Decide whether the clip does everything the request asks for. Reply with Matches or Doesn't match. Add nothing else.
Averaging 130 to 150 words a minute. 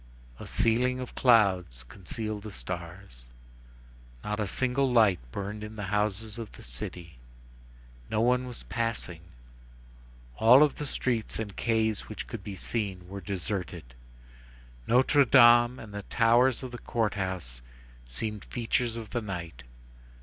Matches